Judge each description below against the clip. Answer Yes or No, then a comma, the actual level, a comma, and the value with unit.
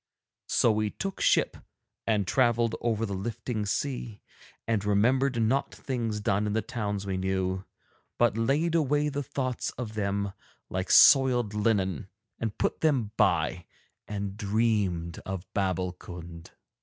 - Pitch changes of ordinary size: Yes, average, 3.5 semitones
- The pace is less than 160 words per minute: Yes, slow, 135 wpm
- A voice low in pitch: Yes, low, 105 Hz